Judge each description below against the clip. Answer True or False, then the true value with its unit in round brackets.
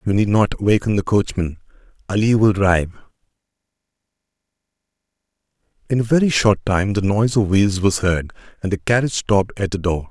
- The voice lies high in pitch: False (100 Hz)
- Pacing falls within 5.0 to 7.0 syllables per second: True (5.9 syllables/s)